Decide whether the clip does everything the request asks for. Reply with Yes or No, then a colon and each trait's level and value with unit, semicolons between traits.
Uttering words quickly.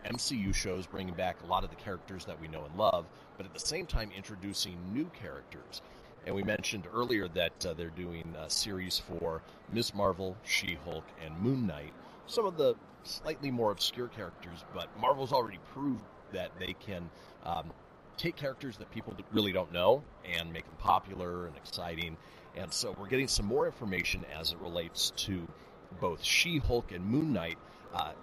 No: average, 180 wpm